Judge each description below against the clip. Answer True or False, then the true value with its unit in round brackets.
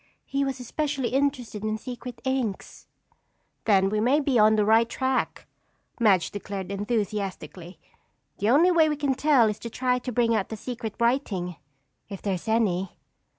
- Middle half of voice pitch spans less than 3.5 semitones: False (4.3 semitones)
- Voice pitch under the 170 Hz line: False (230 Hz)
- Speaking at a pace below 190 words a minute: True (165 wpm)